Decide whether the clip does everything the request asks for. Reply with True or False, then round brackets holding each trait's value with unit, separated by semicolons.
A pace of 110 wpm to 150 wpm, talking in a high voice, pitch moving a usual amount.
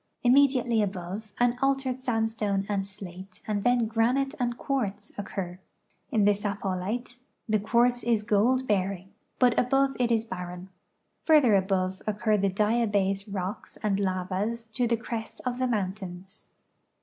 True (140 wpm; 215 Hz; 3.8 semitones)